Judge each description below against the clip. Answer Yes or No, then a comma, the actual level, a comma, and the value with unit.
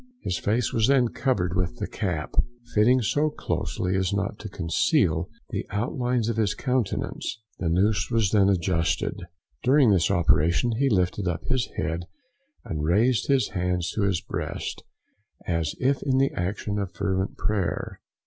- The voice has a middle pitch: No, low, 100 Hz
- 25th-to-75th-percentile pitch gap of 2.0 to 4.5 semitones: No, average, 5.1 semitones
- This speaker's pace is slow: No, average, 160 wpm